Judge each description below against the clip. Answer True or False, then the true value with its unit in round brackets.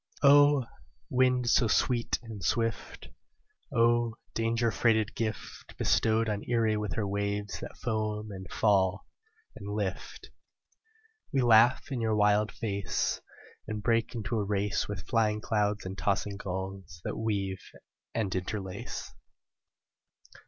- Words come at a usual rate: False (125 wpm)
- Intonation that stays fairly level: True (2.3 semitones)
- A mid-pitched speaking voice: False (105 Hz)